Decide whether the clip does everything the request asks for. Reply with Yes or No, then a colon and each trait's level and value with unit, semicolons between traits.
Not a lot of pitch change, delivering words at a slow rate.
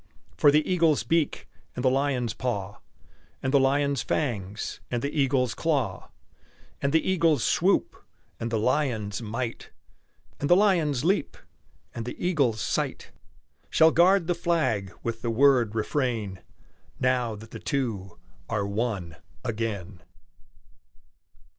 No: average, 5.0 semitones; slow, 130 wpm